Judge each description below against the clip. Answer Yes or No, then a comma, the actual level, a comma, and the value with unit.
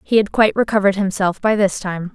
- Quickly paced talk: Yes, fast, 225 wpm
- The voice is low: No, high, 200 Hz